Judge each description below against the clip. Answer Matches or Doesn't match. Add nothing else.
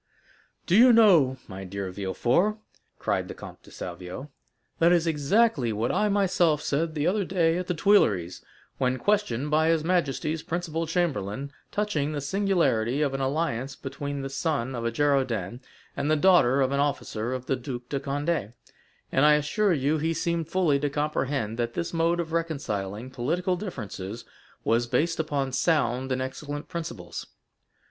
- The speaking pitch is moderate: Matches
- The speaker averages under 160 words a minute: Doesn't match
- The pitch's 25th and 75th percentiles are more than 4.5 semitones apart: Matches